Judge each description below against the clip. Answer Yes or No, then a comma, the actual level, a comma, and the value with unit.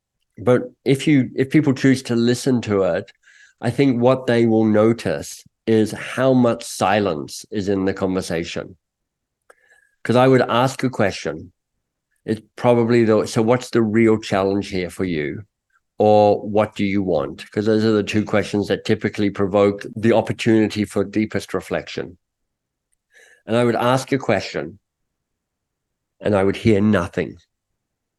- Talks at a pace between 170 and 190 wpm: No, average, 150 wpm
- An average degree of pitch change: Yes, average, 3.4 semitones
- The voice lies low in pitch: Yes, low, 110 Hz